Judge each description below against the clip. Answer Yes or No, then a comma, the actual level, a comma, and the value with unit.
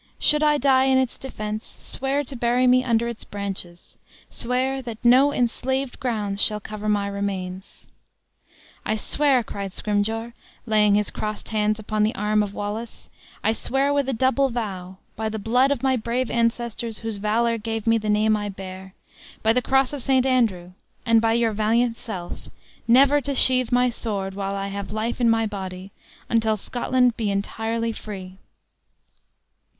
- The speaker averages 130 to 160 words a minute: No, average, 170 wpm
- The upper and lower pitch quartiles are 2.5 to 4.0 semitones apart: Yes, average, 3.3 semitones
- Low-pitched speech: No, high, 225 Hz